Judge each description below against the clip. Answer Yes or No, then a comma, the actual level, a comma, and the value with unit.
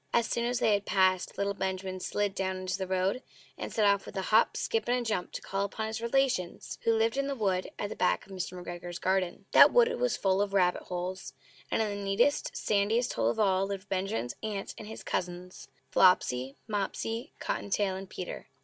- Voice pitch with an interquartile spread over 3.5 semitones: No, average, 2.9 semitones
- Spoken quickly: Yes, fast, 220 wpm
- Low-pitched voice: No, high, 195 Hz